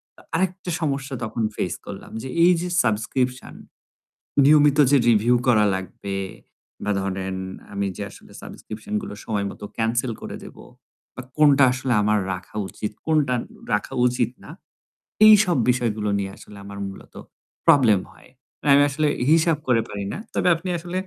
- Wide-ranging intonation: Yes, wide, 6.0 semitones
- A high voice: No, low, 125 Hz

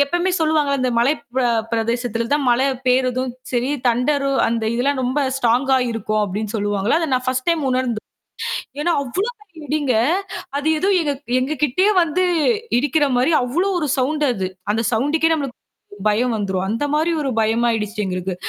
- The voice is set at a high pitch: Yes, very high, 255 Hz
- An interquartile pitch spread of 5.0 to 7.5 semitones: No, average, 4.5 semitones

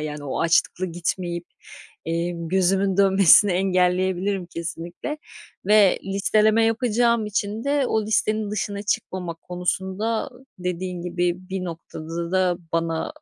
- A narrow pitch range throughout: No, average, 3.1 semitones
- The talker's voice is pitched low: No, medium, 185 Hz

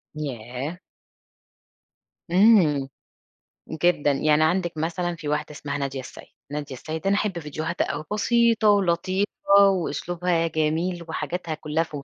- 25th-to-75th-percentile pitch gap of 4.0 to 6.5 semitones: No, average, 3.2 semitones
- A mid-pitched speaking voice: Yes, medium, 165 Hz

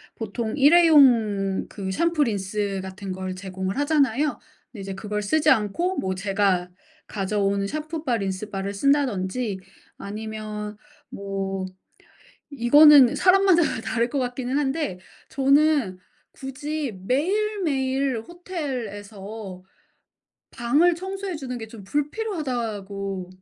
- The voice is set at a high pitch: Yes, high, 235 Hz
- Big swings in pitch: Yes, wide, 6.8 semitones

